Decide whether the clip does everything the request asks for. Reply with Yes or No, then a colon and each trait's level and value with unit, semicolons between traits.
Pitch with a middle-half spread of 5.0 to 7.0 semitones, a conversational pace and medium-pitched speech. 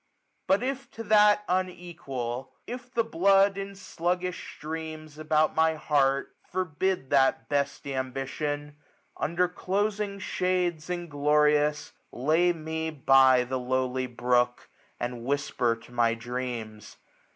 No: wide, 5.6 semitones; slow, 120 wpm; medium, 155 Hz